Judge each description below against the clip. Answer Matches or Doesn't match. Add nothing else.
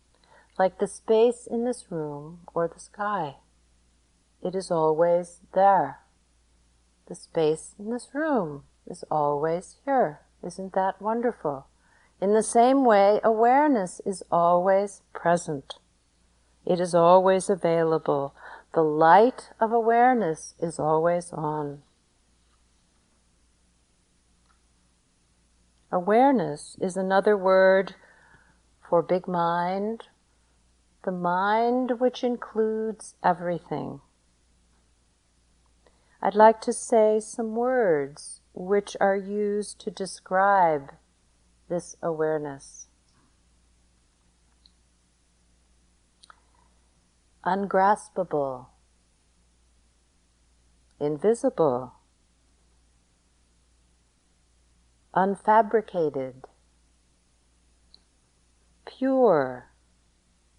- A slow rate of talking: Matches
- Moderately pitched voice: Matches